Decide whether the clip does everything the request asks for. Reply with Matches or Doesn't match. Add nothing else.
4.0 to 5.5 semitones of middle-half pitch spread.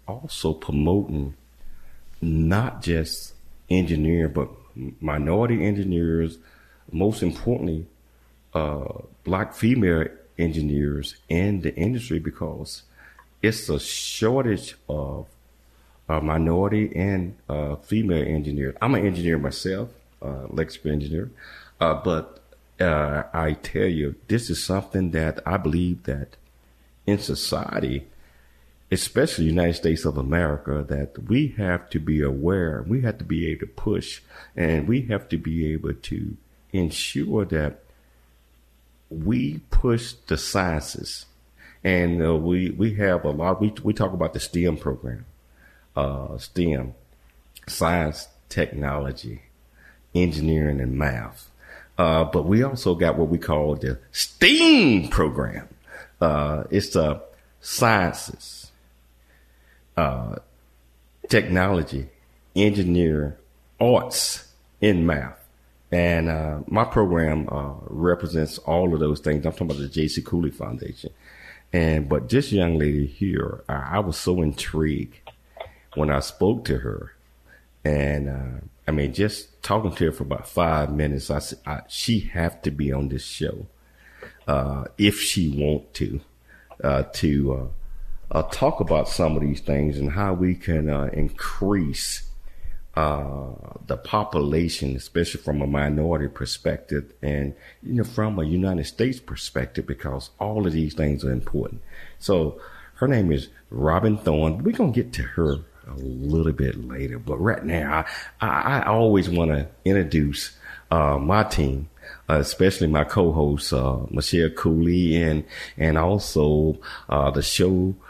Matches